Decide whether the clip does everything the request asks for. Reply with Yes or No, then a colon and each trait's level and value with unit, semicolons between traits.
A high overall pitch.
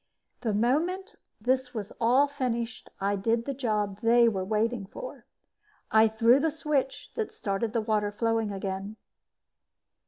Yes: high, 230 Hz